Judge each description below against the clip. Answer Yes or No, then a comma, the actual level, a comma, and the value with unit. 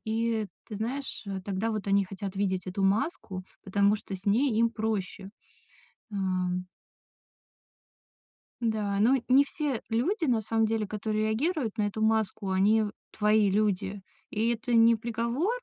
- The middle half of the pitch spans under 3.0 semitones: Yes, narrow, 2.6 semitones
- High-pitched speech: Yes, high, 215 Hz